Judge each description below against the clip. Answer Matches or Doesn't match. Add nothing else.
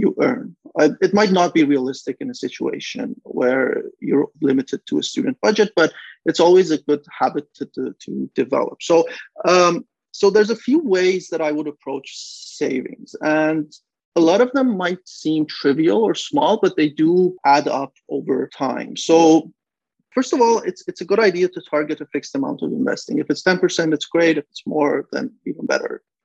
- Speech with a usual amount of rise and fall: Doesn't match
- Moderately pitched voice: Matches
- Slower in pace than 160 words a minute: Doesn't match